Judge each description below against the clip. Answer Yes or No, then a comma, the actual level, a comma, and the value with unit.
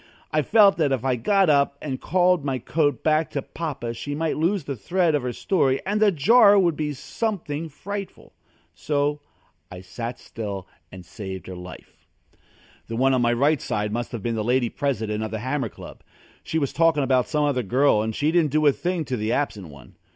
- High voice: No, medium, 140 Hz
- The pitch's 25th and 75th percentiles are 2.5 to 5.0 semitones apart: No, wide, 5.4 semitones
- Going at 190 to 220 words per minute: Yes, fast, 205 wpm